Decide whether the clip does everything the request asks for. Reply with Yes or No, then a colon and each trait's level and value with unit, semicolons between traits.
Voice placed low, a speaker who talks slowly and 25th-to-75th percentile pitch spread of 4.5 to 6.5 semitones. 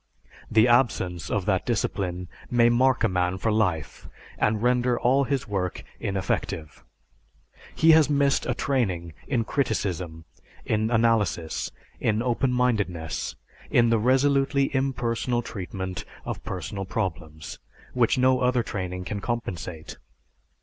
Yes: low, 110 Hz; slow, 125 wpm; wide, 5.4 semitones